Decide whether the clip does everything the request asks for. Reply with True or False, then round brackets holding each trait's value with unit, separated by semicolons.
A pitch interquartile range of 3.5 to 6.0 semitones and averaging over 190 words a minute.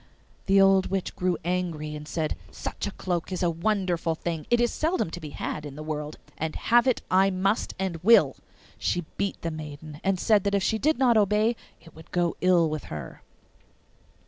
True (4.0 semitones; 200 wpm)